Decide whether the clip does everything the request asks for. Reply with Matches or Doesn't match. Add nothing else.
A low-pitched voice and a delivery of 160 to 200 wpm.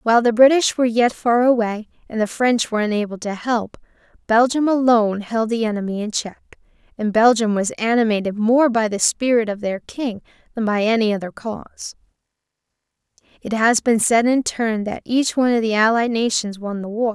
Doesn't match